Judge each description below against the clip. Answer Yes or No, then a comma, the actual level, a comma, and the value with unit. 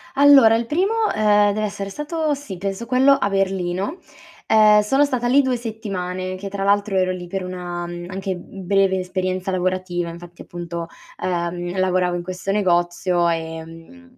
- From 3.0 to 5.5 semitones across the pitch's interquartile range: Yes, average, 3.4 semitones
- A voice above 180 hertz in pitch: Yes, high, 190 Hz